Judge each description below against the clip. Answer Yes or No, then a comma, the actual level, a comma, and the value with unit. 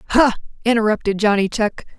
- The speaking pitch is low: No, high, 220 Hz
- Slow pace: Yes, slow, 120 wpm